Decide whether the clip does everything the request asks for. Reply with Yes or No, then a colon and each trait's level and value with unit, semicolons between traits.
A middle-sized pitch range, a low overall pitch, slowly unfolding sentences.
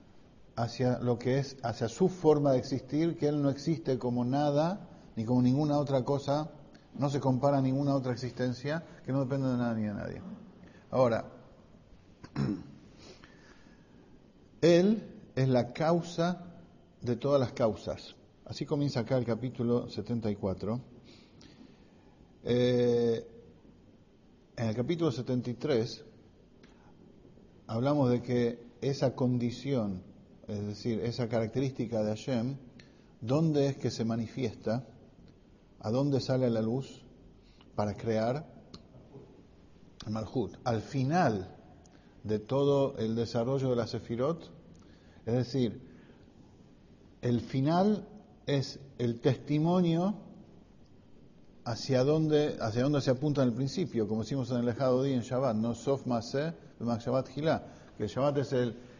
Yes: average, 3.3 semitones; low, 125 Hz; slow, 125 wpm